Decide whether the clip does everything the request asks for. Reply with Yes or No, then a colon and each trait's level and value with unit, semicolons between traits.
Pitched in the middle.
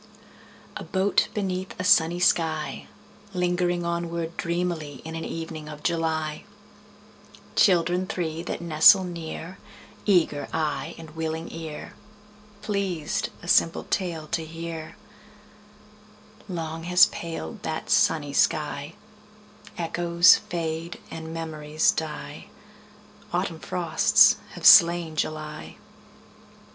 Yes: medium, 165 Hz